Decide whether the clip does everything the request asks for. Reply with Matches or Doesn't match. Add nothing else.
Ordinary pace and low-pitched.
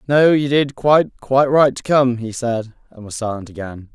Doesn't match